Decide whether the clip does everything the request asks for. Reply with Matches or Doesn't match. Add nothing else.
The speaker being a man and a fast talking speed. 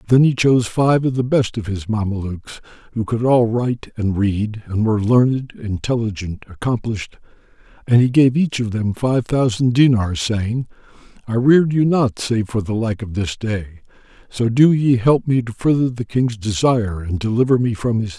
Matches